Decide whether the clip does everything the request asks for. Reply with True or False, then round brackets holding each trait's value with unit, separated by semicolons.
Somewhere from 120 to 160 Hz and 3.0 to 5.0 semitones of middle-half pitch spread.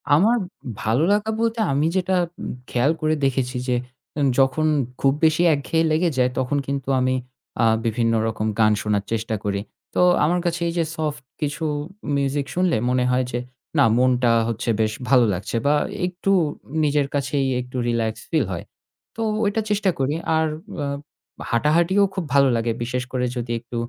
True (135 Hz; 4.7 semitones)